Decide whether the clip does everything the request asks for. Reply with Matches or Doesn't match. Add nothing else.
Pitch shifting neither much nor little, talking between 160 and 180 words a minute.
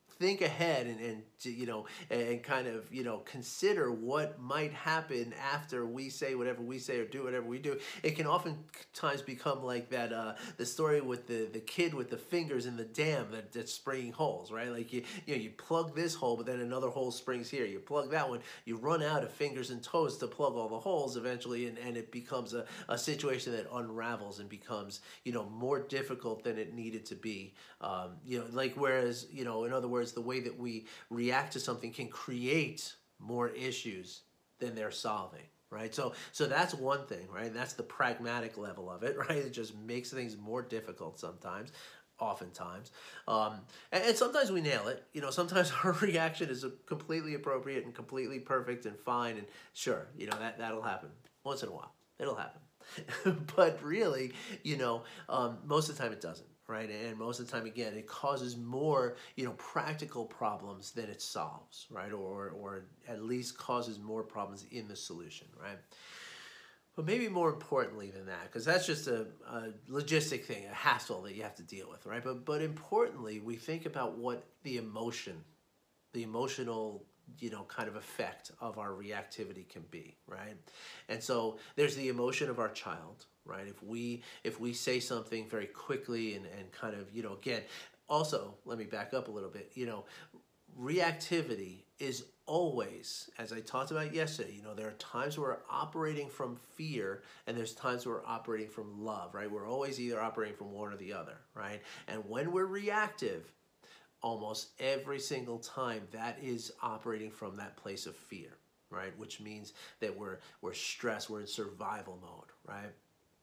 Doesn't match